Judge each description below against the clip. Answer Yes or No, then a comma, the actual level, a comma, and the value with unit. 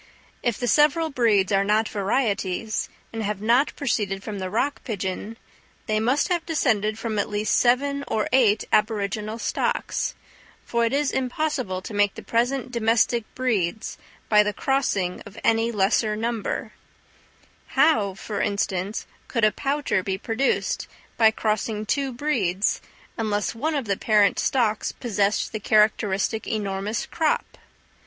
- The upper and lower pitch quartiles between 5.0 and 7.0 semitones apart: No, average, 3.2 semitones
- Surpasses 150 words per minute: No, average, 145 wpm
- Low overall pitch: No, high, 220 Hz